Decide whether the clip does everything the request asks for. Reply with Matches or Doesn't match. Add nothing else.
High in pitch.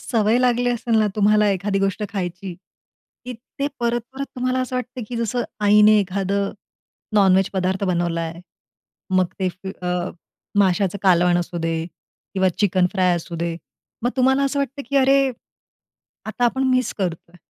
Matches